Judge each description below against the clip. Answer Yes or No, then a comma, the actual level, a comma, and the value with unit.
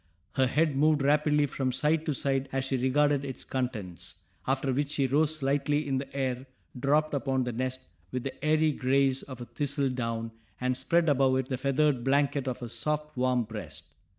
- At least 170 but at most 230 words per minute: Yes, average, 185 wpm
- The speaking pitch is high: No, low, 135 Hz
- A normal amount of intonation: No, narrow, 2.3 semitones